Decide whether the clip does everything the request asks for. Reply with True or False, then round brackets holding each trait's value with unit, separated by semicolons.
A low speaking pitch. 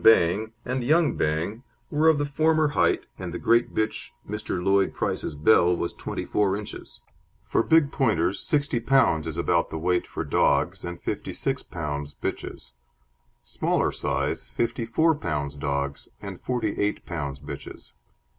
True (100 Hz)